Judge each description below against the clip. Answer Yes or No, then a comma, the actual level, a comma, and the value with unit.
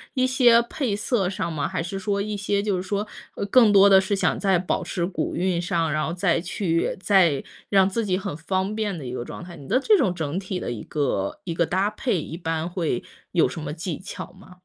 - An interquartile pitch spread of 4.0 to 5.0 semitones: No, average, 3.2 semitones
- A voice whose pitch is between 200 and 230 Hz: No, medium, 185 Hz